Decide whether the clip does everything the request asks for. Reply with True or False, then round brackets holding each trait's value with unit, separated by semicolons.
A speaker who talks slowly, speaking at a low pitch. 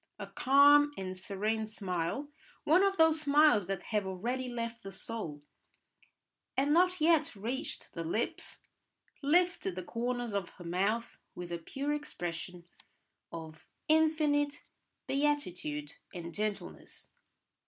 False (120 wpm; 230 Hz)